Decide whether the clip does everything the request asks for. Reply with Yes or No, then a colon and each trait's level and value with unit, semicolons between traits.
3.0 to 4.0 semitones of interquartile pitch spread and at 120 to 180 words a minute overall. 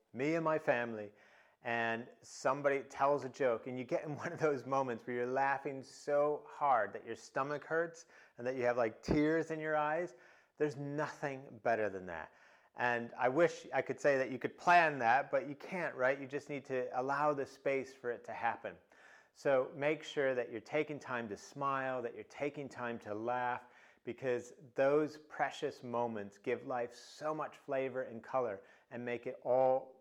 No: average, 3.4 semitones; average, 190 wpm